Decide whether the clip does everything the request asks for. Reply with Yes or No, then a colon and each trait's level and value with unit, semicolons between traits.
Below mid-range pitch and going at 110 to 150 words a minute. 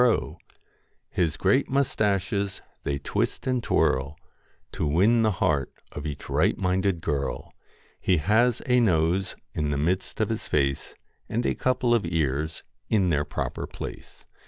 No: very low, 90 Hz; average, 165 wpm